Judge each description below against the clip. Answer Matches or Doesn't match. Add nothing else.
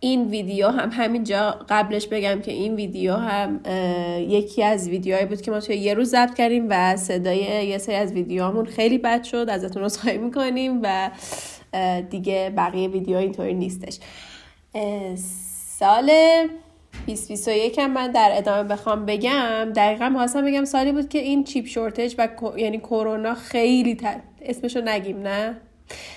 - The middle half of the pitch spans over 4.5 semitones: Doesn't match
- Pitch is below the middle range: Doesn't match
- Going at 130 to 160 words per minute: Matches